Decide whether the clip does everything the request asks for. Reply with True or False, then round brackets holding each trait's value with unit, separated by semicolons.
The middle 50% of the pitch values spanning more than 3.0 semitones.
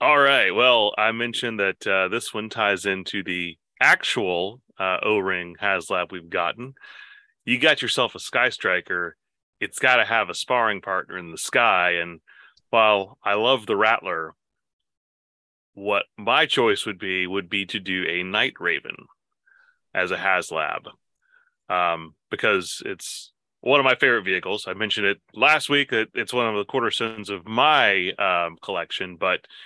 True (5.0 semitones)